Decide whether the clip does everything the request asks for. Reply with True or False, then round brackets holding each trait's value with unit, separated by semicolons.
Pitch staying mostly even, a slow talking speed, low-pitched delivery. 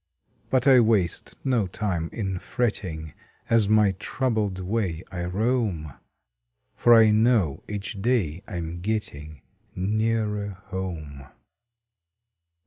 False (4.3 semitones; 110 wpm; 100 Hz)